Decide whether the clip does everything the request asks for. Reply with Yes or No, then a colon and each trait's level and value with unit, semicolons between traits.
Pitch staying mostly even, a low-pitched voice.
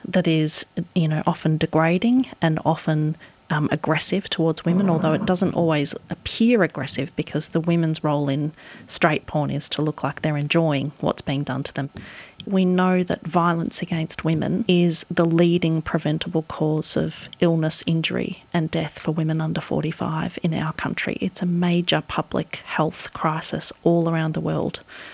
No: narrow, 2.2 semitones; medium, 160 Hz